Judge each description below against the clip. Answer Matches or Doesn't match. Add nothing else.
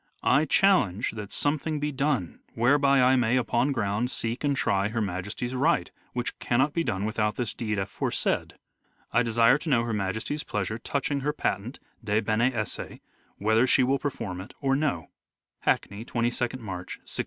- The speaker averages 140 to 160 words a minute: Doesn't match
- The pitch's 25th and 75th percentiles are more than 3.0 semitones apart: Matches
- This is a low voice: Matches